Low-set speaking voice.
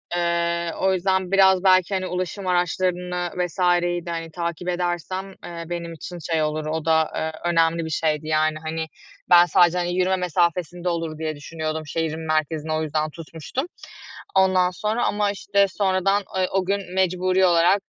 No: medium, 175 Hz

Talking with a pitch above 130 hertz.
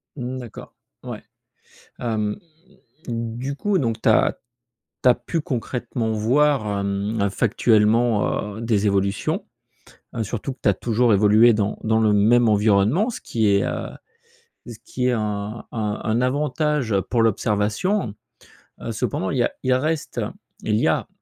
No: low, 115 Hz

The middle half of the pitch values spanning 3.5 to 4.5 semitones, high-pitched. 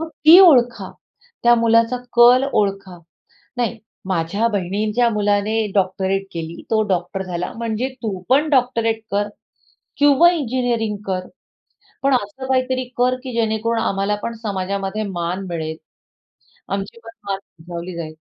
Yes: average, 4.1 semitones; high, 215 Hz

